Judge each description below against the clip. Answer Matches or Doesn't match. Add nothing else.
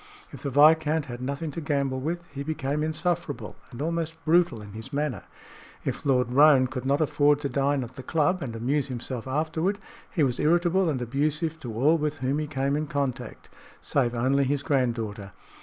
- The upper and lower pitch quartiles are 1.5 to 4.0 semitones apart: Matches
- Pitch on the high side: Doesn't match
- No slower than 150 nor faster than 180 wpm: Doesn't match